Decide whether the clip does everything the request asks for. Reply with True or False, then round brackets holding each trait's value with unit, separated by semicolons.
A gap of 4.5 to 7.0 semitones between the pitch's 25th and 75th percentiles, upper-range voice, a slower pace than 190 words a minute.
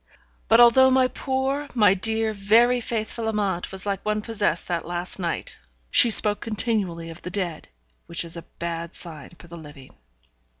True (4.9 semitones; 205 Hz; 170 wpm)